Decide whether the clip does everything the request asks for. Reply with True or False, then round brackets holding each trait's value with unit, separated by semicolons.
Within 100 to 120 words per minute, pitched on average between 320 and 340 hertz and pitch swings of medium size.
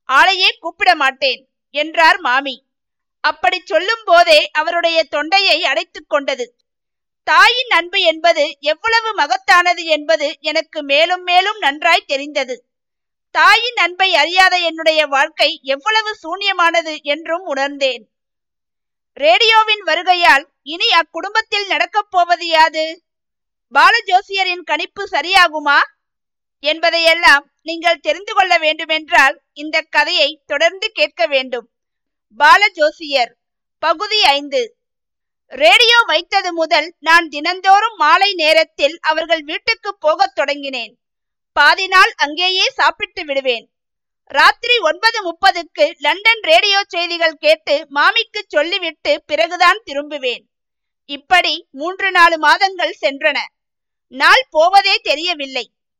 False (90 wpm; 330 Hz; 4.0 semitones)